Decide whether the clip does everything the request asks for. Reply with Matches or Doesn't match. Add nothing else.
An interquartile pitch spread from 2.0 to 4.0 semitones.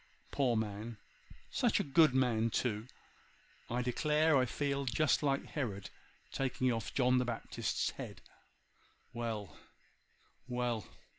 Matches